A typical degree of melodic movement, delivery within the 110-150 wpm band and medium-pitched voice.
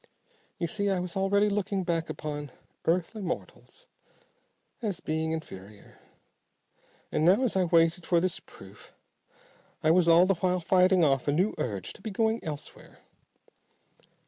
Yes: average, 3.3 semitones; average, 145 wpm; medium, 175 Hz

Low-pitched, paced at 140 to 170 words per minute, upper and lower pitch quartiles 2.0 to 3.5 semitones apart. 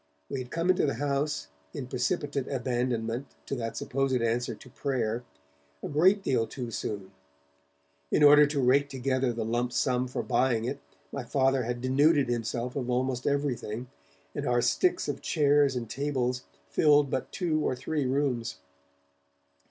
Yes: low, 130 Hz; average, 160 wpm; average, 2.8 semitones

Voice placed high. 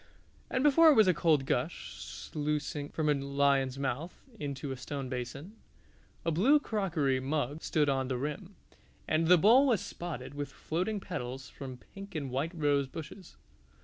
No: medium, 150 Hz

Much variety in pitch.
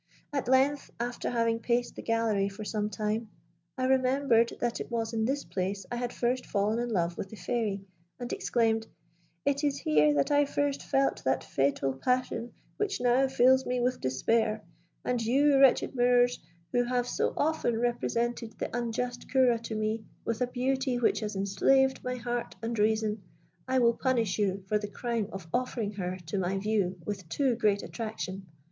No: average, 3.2 semitones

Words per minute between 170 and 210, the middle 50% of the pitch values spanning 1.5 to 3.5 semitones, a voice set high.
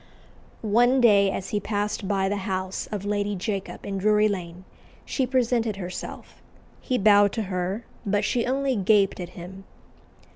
No: average, 155 wpm; narrow, 2.5 semitones; high, 205 Hz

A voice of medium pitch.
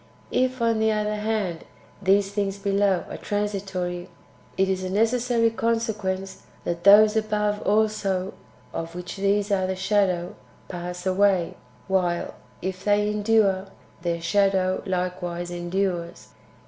No: high, 195 Hz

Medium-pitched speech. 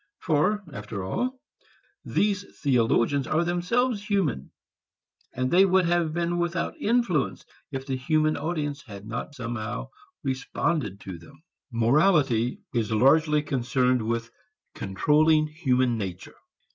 Yes: medium, 145 Hz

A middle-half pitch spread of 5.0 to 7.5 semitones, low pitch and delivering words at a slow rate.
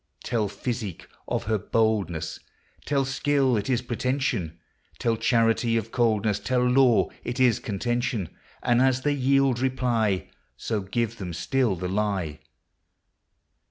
No: average, 3.8 semitones; low, 115 Hz; slow, 130 wpm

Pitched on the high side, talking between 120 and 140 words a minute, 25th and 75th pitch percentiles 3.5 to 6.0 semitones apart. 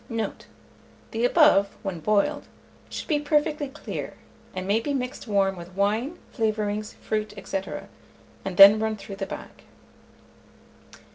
Yes: high, 215 Hz; slow, 135 wpm; average, 4.7 semitones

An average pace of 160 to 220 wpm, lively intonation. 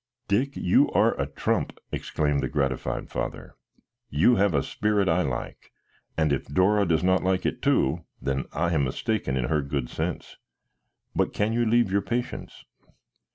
Yes: average, 165 wpm; wide, 6.2 semitones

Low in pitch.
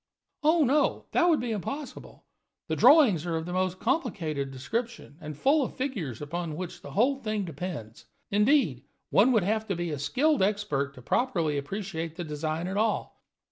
No: high, 190 Hz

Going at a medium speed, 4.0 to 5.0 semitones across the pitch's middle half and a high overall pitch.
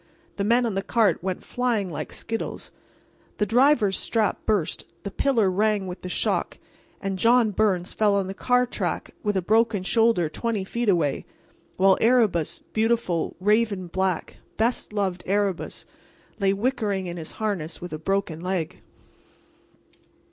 No: average, 145 wpm; average, 3.4 semitones; high, 200 Hz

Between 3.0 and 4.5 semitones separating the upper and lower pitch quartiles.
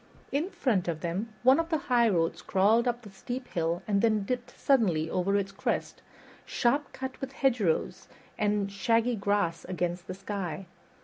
No: average, 4.9 semitones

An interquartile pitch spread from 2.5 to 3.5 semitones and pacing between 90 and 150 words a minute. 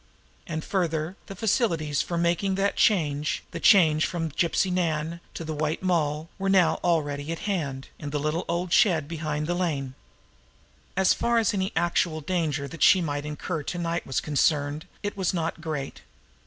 No: average, 3.1 semitones; average, 180 wpm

